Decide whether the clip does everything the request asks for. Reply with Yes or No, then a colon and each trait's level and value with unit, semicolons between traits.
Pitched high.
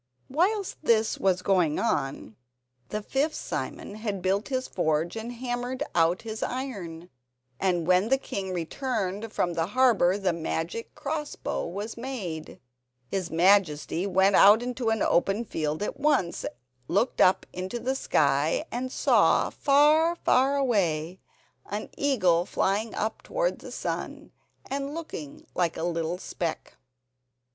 Yes: high, 200 Hz